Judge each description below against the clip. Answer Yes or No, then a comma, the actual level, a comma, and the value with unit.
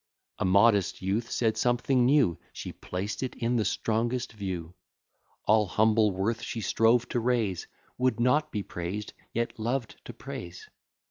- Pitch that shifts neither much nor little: Yes, average, 3.4 semitones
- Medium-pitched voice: No, low, 110 Hz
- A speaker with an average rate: Yes, average, 150 wpm